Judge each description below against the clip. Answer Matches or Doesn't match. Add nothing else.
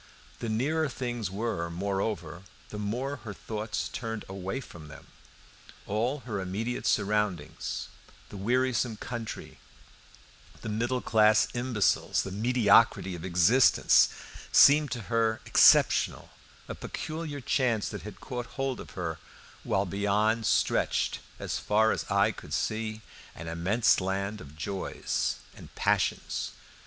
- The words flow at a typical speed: Doesn't match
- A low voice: Matches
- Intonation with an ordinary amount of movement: Matches